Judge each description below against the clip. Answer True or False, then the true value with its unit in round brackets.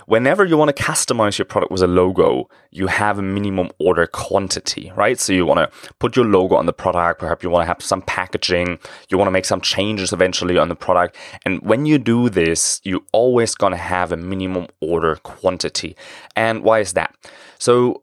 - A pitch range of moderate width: True (3.9 semitones)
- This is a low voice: True (95 Hz)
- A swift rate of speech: True (210 wpm)